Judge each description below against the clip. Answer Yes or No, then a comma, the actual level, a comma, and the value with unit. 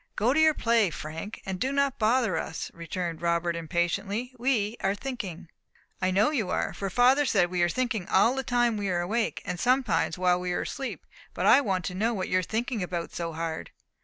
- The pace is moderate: No, fast, 215 wpm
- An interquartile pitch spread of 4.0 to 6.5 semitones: Yes, wide, 5.6 semitones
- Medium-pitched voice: No, high, 200 Hz